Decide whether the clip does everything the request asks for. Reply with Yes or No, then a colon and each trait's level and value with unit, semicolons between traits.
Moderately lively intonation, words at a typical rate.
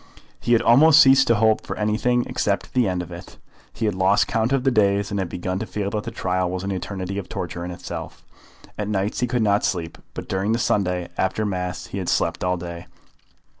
No: average, 3.4 semitones; fast, 230 wpm